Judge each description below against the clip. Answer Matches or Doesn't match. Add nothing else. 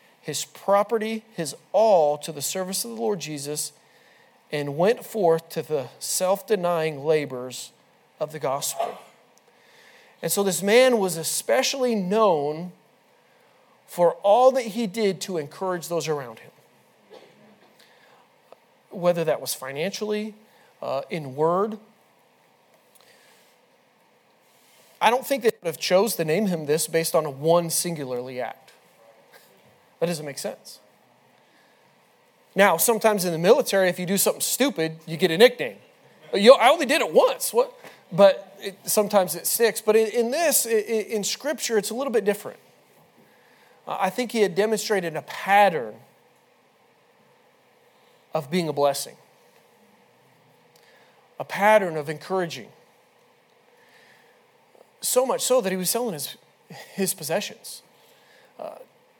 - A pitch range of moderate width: Doesn't match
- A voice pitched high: Matches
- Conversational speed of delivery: Doesn't match